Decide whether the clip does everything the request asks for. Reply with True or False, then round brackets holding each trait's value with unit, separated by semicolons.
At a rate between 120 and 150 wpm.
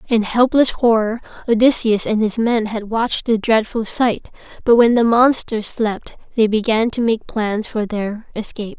False (170 wpm)